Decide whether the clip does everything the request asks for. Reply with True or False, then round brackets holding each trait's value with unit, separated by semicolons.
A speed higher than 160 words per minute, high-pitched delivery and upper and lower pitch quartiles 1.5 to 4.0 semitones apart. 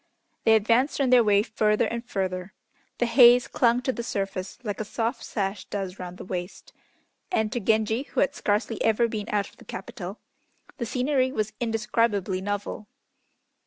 True (170 wpm; 220 Hz; 2.9 semitones)